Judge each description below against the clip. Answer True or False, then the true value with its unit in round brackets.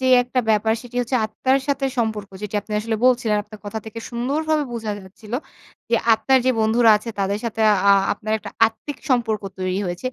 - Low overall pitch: False (225 Hz)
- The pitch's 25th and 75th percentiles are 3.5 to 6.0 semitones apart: False (2.9 semitones)